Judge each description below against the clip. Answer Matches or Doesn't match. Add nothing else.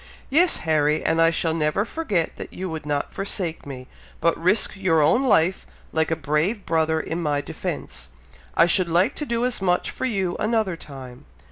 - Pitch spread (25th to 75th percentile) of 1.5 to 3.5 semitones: Doesn't match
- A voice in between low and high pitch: Matches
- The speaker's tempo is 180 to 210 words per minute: Matches